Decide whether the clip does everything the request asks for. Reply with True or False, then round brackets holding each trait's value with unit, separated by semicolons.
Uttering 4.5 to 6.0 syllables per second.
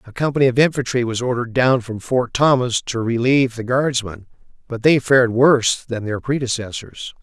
True (5.5 syllables/s)